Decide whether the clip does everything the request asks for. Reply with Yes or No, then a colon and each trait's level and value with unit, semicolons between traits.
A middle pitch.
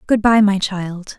No: high, 200 Hz